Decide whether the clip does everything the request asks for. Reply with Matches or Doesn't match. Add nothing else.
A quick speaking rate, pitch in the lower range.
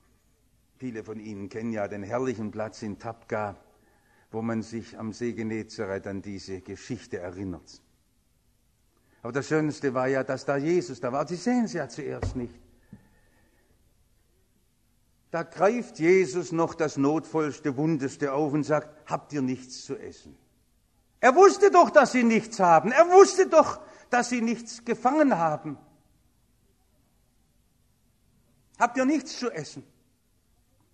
Doesn't match